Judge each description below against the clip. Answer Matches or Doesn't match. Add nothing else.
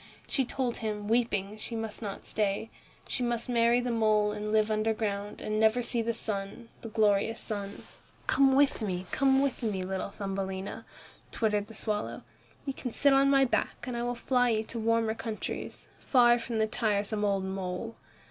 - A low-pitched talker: Doesn't match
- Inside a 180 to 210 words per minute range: Matches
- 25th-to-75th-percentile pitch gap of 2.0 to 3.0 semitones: Matches